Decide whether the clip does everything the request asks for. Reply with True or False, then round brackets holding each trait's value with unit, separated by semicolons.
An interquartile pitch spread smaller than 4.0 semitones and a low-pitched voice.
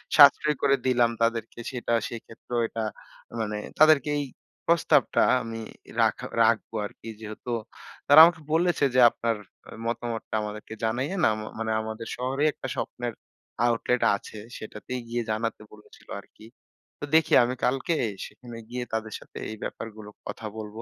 True (3.0 semitones; 115 Hz)